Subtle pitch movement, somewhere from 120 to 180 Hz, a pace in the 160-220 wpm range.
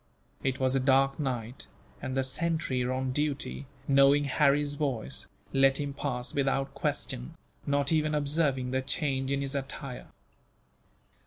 No: narrow, 1.6 semitones; low, 135 Hz; average, 140 wpm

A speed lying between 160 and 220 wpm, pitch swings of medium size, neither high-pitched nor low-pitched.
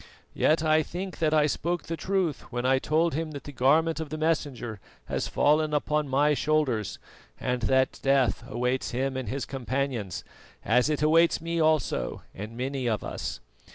Yes: average, 170 wpm; average, 3.4 semitones; medium, 145 Hz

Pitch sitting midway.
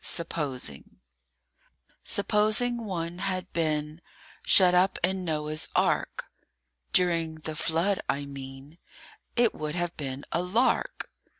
Yes: medium, 170 Hz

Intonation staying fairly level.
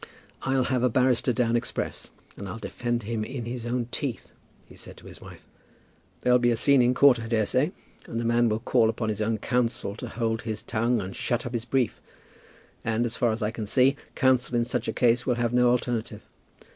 Yes: narrow, 1.7 semitones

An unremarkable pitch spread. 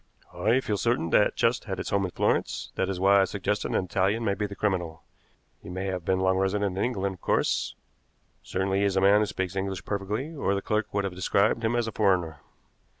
No: narrow, 1.9 semitones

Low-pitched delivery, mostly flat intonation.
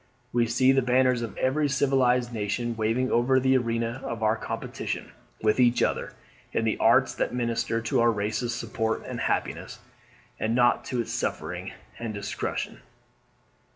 Yes: low, 120 Hz; narrow, 2.1 semitones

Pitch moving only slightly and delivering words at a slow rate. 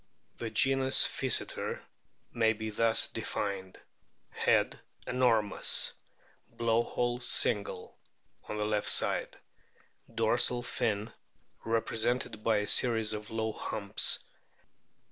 Yes: narrow, 2.2 semitones; slow, 95 wpm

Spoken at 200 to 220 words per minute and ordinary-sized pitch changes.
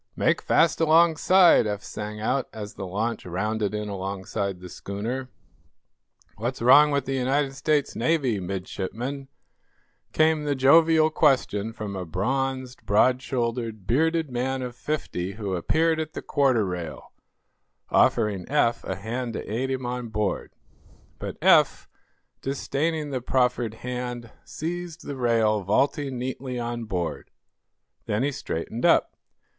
No: slow, 135 wpm; average, 4.8 semitones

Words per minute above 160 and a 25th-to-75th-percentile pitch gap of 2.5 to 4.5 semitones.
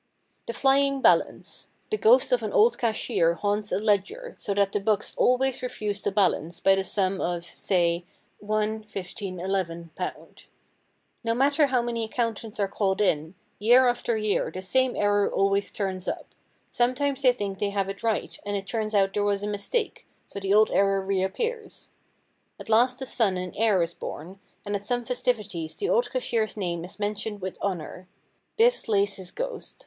Yes: average, 175 wpm; average, 4.0 semitones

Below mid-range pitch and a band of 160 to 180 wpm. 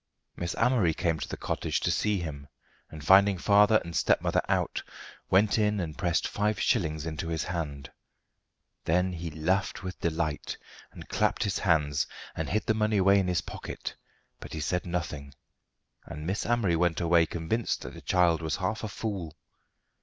Yes: very low, 85 Hz; average, 175 wpm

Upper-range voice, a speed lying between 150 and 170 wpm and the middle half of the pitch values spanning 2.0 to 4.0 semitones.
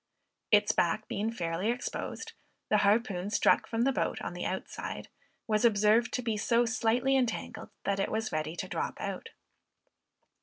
Yes: high, 220 Hz; average, 160 wpm; average, 2.7 semitones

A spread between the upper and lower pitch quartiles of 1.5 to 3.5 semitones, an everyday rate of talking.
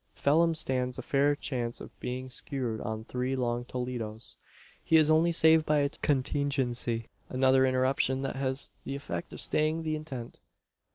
Yes: average, 2.8 semitones; average, 160 wpm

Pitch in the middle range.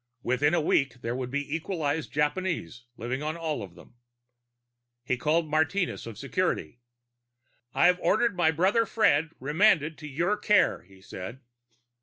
Yes: medium, 150 Hz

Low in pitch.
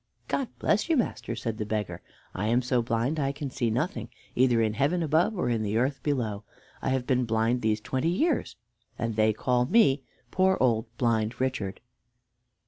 Yes: low, 125 Hz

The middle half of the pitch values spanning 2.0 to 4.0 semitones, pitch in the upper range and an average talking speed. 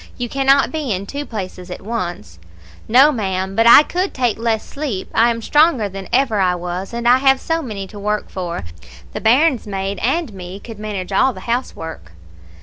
No: wide, 5.5 semitones; high, 220 Hz; average, 195 wpm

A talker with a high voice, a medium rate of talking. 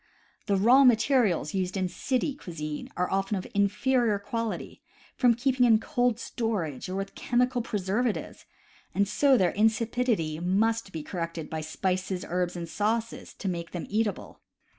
Yes: high, 205 Hz; average, 145 wpm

